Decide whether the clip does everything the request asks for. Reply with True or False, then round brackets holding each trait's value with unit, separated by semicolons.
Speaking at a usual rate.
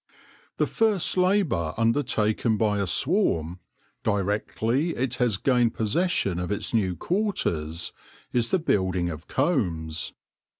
False (120 wpm)